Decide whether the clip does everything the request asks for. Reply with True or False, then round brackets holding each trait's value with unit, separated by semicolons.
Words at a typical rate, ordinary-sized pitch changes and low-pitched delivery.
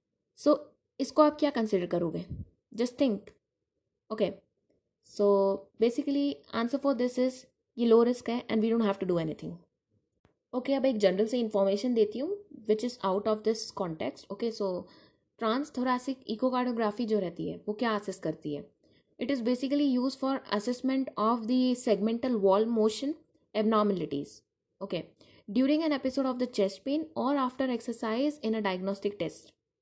False (165 wpm; 4.5 semitones; 230 Hz)